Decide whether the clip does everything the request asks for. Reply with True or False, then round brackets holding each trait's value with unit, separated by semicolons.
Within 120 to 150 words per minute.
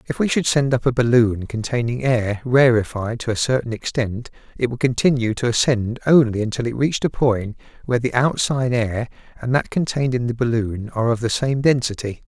False (195 wpm)